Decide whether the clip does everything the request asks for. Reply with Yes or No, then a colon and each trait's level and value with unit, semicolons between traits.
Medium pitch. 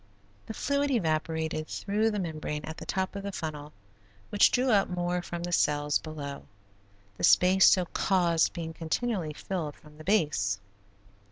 Yes: medium, 170 Hz